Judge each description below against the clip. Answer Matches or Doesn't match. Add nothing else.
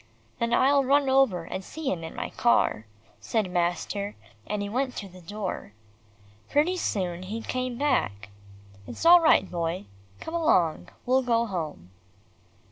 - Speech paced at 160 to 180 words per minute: Doesn't match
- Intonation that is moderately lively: Doesn't match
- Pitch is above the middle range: Matches